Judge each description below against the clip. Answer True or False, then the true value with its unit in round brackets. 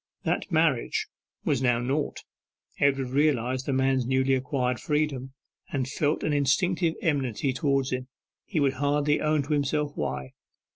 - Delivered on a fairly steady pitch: True (2.3 semitones)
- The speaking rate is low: False (145 wpm)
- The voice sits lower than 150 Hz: True (140 Hz)